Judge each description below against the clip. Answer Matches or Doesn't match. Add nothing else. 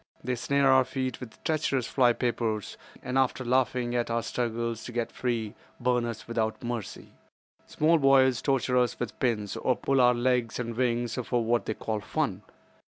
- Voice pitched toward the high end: Doesn't match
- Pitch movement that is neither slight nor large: Doesn't match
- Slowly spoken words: Doesn't match